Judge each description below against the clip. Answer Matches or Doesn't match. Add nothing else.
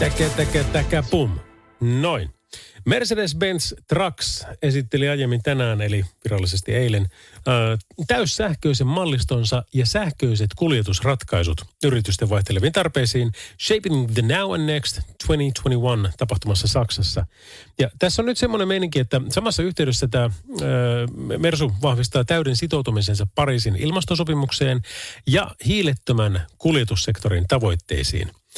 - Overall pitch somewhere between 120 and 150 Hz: Matches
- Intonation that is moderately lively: Doesn't match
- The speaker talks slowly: Doesn't match